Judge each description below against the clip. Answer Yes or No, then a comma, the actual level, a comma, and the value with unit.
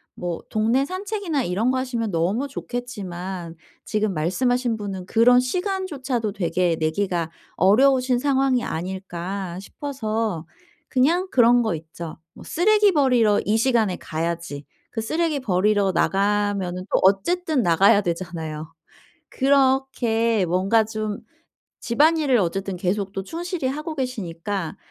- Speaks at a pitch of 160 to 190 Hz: No, high, 215 Hz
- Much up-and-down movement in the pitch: Yes, wide, 6.3 semitones